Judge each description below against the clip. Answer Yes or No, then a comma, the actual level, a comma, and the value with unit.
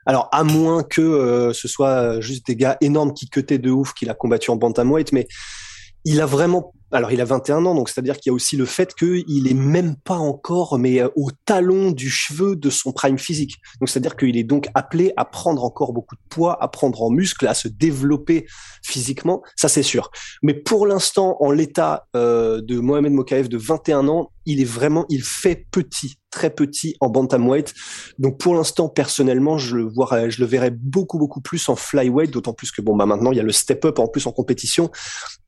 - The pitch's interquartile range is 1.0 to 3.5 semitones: No, average, 4.0 semitones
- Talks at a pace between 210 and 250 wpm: Yes, average, 215 wpm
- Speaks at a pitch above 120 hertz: Yes, medium, 140 Hz